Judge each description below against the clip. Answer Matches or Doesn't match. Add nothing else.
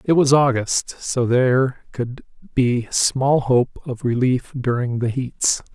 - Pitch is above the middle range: Doesn't match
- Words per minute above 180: Doesn't match